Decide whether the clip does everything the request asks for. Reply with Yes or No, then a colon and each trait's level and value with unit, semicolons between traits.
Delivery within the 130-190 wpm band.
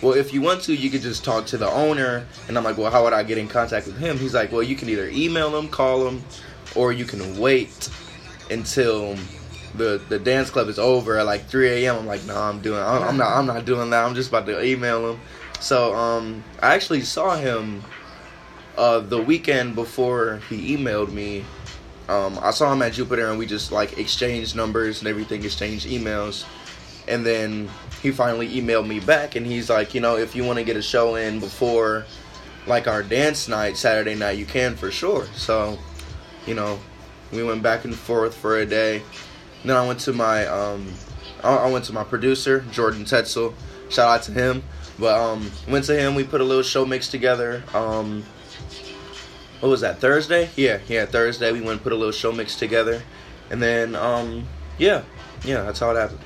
No: fast, 205 wpm